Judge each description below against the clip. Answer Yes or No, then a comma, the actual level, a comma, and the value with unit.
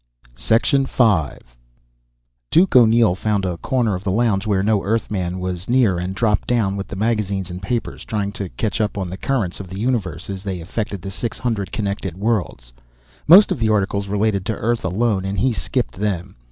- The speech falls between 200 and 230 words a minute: No, average, 190 wpm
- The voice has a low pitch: Yes, low, 100 Hz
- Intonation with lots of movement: No, average, 3.2 semitones